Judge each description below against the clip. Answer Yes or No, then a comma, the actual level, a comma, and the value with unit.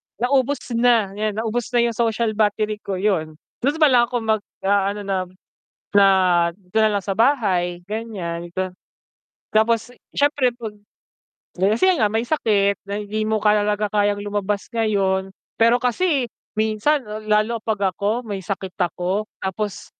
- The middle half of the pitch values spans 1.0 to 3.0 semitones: Yes, average, 2.7 semitones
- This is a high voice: Yes, high, 215 Hz